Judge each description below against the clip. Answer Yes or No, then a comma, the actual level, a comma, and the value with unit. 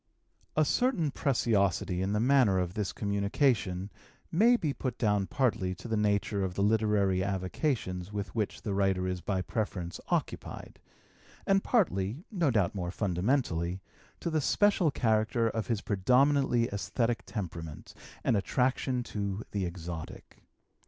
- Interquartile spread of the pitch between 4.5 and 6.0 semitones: Yes, average, 5.1 semitones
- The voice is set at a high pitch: No, low, 105 Hz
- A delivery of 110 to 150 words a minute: Yes, average, 140 wpm